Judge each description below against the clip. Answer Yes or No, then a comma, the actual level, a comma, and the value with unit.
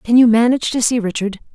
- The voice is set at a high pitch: Yes, high, 230 Hz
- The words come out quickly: Yes, fast, 230 wpm